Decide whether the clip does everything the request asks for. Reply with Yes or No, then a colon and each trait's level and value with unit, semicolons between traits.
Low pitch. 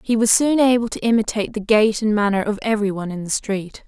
No: high, 215 Hz